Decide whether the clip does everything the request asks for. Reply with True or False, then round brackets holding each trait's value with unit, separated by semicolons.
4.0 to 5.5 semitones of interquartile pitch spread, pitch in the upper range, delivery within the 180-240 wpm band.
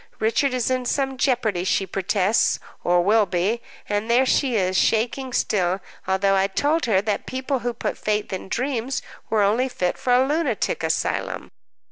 False (4.7 semitones; 225 Hz; 170 wpm)